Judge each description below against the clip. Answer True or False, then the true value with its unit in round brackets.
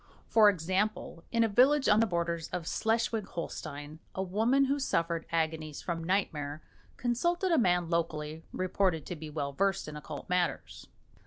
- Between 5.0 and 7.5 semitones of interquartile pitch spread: True (5.4 semitones)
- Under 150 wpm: False (160 wpm)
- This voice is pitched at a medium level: True (180 Hz)